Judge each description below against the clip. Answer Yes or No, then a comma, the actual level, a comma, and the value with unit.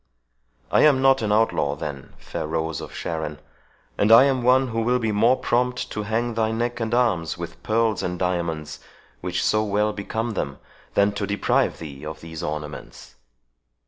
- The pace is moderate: Yes, average, 175 wpm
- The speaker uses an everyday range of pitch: No, wide, 6.3 semitones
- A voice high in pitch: No, low, 105 Hz